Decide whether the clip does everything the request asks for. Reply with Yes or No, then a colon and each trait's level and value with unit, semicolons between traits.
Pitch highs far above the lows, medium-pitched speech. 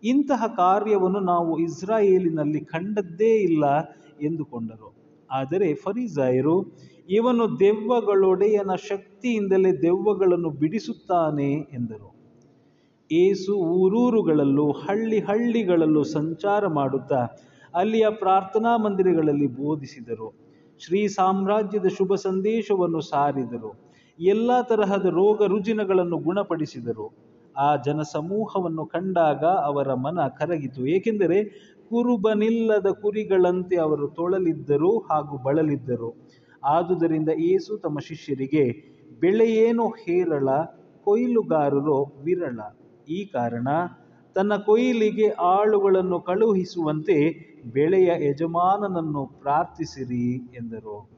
Yes: wide, 5.8 semitones; medium, 175 Hz